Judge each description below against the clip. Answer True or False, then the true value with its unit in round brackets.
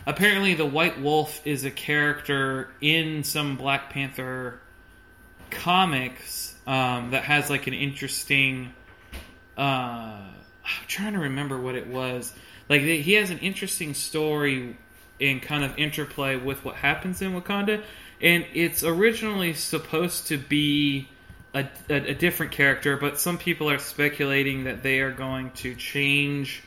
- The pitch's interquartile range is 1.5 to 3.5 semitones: True (3.2 semitones)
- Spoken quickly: False (140 wpm)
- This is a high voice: False (140 Hz)